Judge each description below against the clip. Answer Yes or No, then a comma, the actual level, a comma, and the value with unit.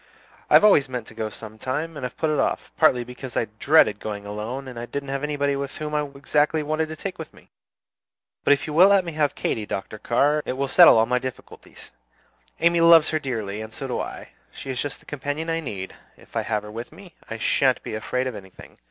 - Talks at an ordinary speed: No, fast, 235 wpm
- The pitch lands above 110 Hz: Yes, low, 135 Hz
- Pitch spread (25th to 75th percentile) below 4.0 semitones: No, average, 4.8 semitones